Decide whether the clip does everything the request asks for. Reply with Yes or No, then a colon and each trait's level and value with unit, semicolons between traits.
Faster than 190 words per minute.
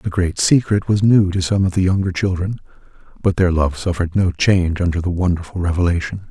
Yes: average, 200 wpm